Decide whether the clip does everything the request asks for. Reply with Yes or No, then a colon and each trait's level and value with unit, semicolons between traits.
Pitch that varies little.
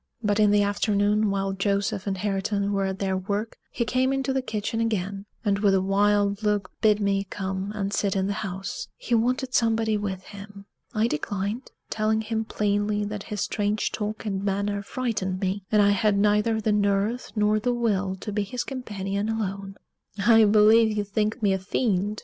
Yes: narrow, 1.6 semitones